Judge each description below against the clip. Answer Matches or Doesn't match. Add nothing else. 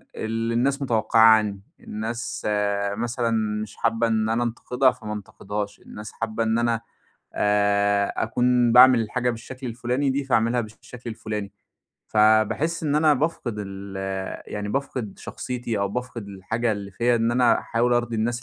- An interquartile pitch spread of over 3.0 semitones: Doesn't match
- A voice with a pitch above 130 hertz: Doesn't match